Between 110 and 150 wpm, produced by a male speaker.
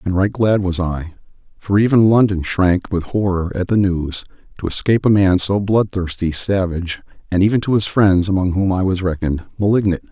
No: average, 180 wpm; male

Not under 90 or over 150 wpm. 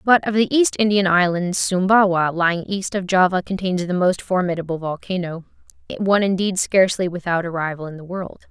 No: average, 170 wpm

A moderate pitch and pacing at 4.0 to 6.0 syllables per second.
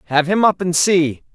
Yes: medium, 175 Hz; 4.7 syllables/s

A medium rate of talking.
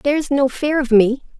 No: fast, 215 wpm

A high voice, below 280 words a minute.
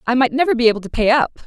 No: high, 245 Hz; fast, 330 wpm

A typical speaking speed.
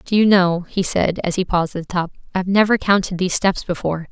No: fast, 250 wpm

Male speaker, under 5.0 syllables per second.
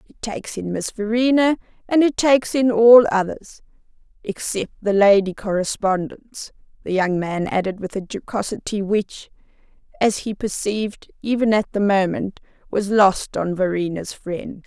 No: female; 4.6 syllables/s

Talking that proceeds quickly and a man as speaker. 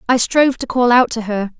No: fast, 265 wpm; female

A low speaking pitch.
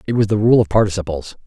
Yes: low, 100 Hz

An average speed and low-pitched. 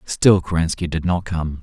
Yes: average, 185 wpm; very low, 85 Hz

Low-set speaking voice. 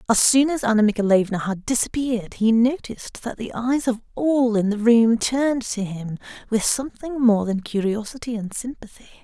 No: high, 230 Hz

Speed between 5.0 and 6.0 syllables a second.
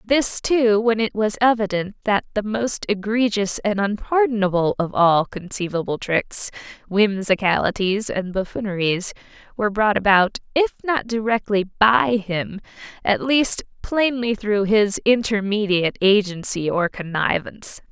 No: 4.3 syllables/s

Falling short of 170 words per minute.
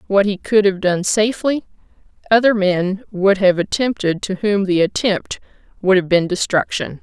Yes: average, 160 wpm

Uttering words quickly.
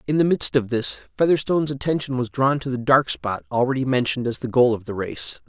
Yes: fast, 230 wpm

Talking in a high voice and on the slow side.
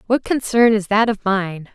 No: high, 215 Hz; fast, 205 wpm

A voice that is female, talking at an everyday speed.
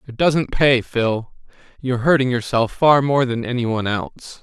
No: male; average, 175 wpm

